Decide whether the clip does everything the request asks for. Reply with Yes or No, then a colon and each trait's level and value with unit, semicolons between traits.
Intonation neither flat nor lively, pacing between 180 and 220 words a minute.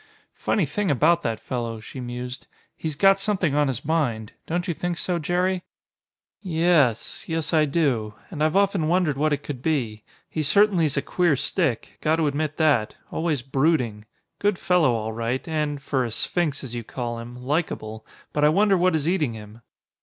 No: wide, 5.7 semitones; average, 185 wpm